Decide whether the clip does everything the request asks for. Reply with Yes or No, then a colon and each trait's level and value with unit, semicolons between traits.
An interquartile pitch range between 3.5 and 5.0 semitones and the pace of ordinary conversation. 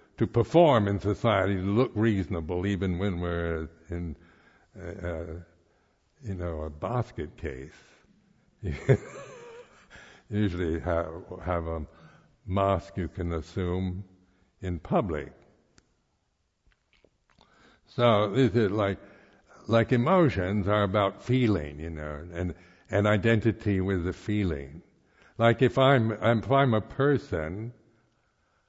No: average, 4.5 semitones; slow, 110 wpm